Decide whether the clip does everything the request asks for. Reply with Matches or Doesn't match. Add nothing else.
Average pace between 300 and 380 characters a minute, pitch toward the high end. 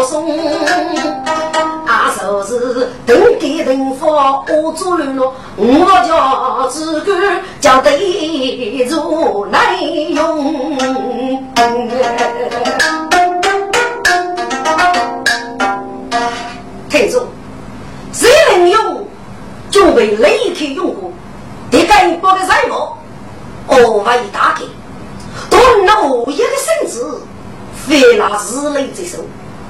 Doesn't match